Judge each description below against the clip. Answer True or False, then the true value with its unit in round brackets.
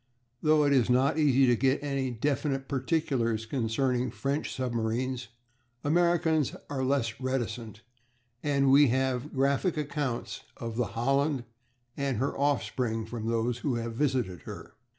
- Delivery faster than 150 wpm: False (135 wpm)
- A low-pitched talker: True (130 Hz)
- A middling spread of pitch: True (3.2 semitones)